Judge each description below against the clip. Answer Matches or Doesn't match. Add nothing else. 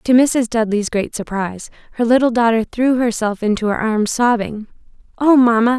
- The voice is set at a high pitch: Matches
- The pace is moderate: Matches